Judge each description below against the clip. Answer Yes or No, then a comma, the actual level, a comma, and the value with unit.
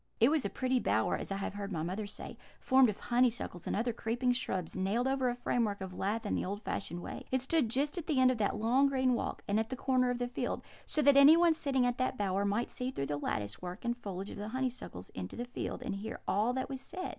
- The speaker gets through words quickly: Yes, fast, 260 wpm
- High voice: Yes, high, 240 Hz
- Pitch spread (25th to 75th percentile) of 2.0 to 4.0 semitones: No, average, 4.4 semitones